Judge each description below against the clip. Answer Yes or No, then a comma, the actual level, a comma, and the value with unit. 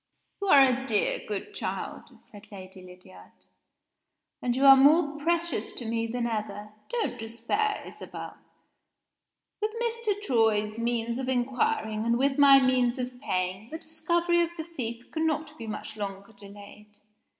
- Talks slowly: No, average, 150 wpm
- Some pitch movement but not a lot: No, wide, 5.8 semitones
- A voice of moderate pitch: No, high, 240 Hz